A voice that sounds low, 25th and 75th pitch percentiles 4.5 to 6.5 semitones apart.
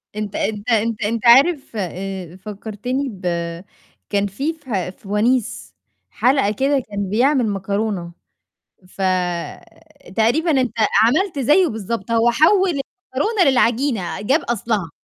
No: high, 230 Hz; average, 5.1 semitones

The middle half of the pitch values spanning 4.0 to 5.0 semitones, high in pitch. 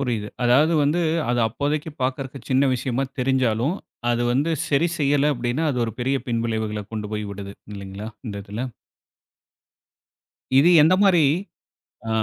No: average, 4.4 semitones; low, 125 Hz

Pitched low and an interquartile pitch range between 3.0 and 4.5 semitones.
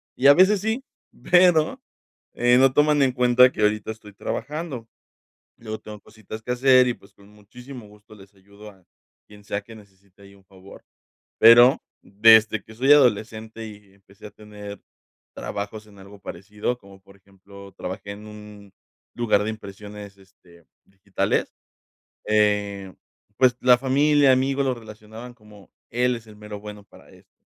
Yes: low, 105 Hz; average, 3.5 semitones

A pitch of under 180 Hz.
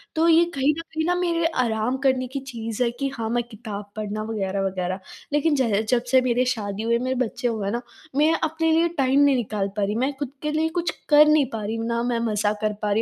No: high, 245 Hz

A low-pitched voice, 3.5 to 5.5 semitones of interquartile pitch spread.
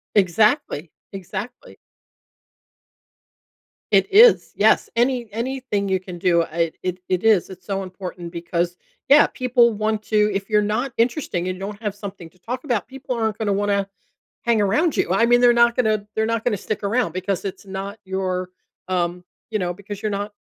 No: high, 205 Hz; average, 3.9 semitones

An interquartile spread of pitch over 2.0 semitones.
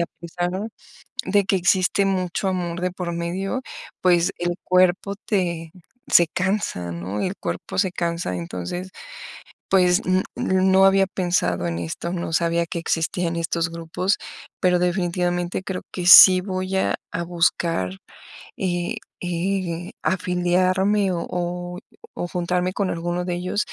No: narrow, 1.5 semitones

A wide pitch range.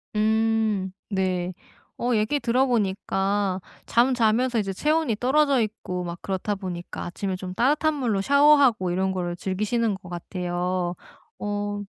No: average, 4.4 semitones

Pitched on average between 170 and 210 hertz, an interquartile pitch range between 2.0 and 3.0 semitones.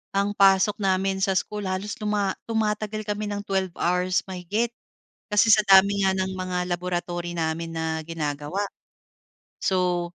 Yes: high, 190 Hz; average, 2.7 semitones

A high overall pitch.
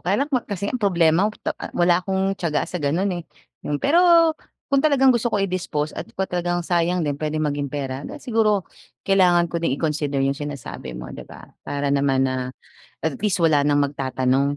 No: medium, 170 Hz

